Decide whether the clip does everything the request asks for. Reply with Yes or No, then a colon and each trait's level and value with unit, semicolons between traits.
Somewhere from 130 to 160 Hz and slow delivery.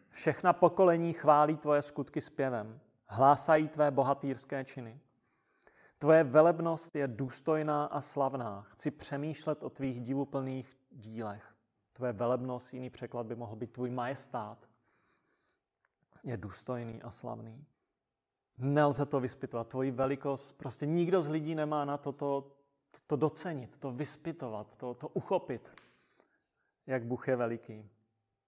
No: low, 135 Hz; average, 125 wpm